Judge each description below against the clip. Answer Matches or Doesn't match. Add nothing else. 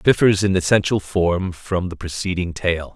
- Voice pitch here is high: Doesn't match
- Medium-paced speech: Matches